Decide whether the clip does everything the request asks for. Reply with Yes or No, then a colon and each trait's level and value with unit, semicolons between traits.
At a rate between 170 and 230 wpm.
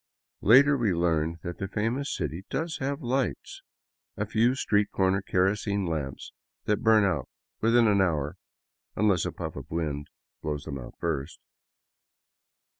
No: average, 150 wpm